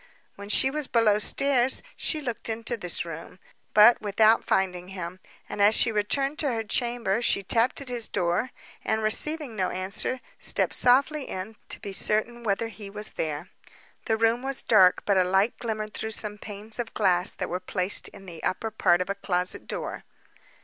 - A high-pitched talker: Yes, high, 215 Hz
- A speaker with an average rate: Yes, average, 185 wpm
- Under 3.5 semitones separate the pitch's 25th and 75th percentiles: No, average, 3.8 semitones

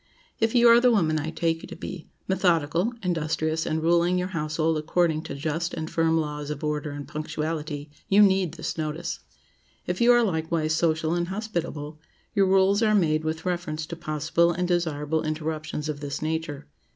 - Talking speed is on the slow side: No, average, 175 wpm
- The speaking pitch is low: No, medium, 160 Hz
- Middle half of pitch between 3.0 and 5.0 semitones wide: No, narrow, 2.4 semitones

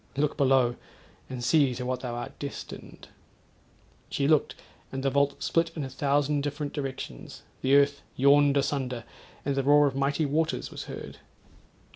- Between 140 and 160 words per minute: Yes, average, 155 wpm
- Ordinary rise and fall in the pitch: No, narrow, 1.6 semitones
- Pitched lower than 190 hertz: Yes, medium, 140 Hz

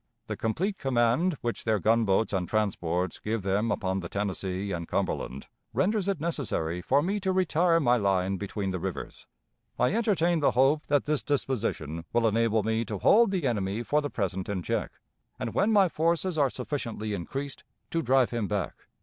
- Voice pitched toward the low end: Yes, low, 115 Hz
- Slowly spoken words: No, average, 180 wpm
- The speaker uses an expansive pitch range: Yes, wide, 7.6 semitones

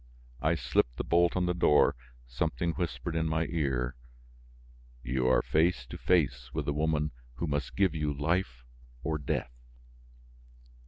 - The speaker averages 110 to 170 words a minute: Yes, average, 150 wpm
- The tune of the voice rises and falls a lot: No, average, 4.7 semitones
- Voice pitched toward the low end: Yes, very low, 75 Hz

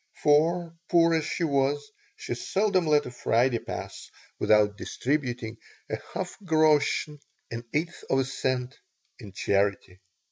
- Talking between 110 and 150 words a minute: Yes, average, 140 wpm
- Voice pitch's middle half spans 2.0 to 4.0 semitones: No, average, 4.7 semitones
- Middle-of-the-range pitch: Yes, medium, 145 Hz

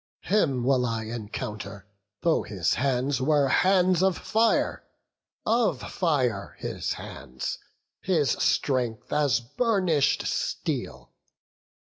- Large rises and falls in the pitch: Yes, wide, 7.6 semitones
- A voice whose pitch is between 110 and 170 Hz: Yes, low, 135 Hz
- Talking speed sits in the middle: No, slow, 100 wpm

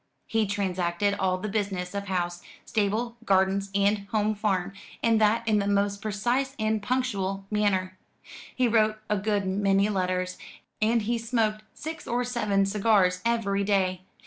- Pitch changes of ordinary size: No, narrow, 2.2 semitones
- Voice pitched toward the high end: Yes, high, 205 Hz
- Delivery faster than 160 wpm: No, average, 150 wpm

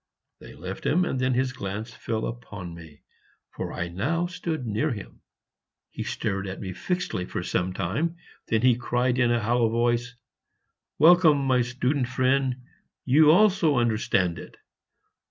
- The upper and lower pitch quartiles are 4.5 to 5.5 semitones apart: Yes, average, 5.0 semitones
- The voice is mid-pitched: No, low, 125 Hz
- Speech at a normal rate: Yes, average, 155 wpm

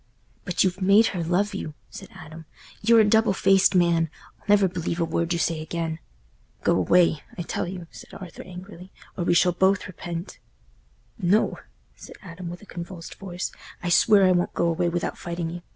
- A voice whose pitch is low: No, medium, 175 Hz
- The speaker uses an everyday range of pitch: No, narrow, 2.2 semitones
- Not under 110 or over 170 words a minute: No, average, 185 wpm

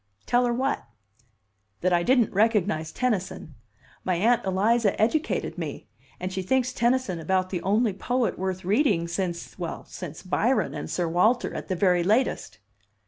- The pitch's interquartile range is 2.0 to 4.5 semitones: No, average, 5.0 semitones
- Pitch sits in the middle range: No, high, 195 Hz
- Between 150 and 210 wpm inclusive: Yes, average, 155 wpm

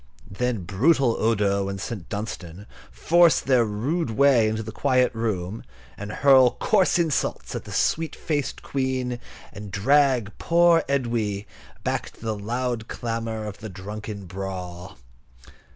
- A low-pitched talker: Yes, low, 115 Hz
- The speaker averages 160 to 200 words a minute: No, slow, 135 wpm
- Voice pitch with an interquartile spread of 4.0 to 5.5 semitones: Yes, average, 4.6 semitones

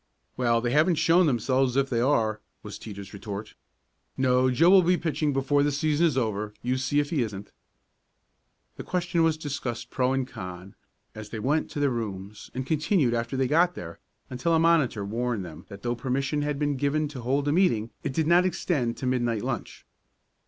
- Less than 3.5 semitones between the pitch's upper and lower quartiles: No, average, 4.5 semitones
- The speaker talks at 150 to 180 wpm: No, average, 195 wpm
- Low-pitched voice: Yes, low, 130 Hz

